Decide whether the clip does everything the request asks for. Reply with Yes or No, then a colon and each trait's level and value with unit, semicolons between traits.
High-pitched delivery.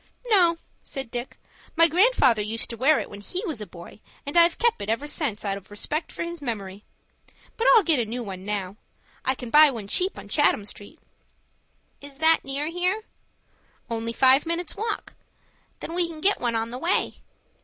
Yes: very high, 275 Hz